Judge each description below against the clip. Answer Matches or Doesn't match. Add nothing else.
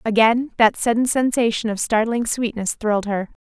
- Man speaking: Doesn't match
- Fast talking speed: Doesn't match